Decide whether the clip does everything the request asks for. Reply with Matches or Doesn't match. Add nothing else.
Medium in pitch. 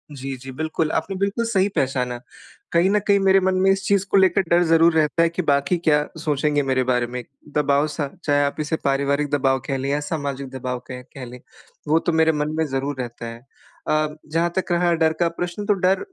Matches